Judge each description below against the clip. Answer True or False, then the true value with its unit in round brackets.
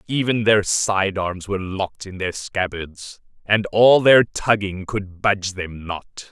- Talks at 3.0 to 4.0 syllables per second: True (3.9 syllables/s)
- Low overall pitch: True (95 Hz)